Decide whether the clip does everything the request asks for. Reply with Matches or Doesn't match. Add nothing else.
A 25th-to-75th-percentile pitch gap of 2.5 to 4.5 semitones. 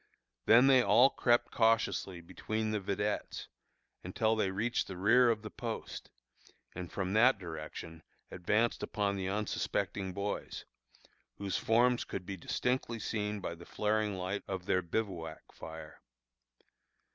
Matches